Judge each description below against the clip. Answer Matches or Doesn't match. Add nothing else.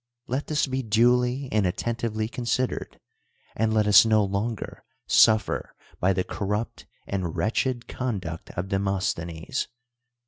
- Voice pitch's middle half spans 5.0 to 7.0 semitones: Doesn't match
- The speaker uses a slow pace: Matches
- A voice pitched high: Doesn't match